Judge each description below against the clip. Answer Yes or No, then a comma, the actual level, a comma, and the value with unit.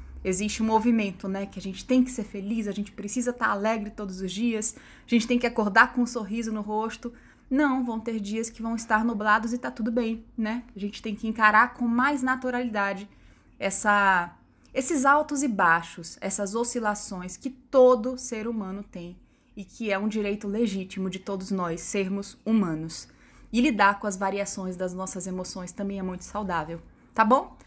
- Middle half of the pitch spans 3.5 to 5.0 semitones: No, average, 3.1 semitones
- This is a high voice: Yes, high, 215 Hz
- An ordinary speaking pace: No, fast, 190 wpm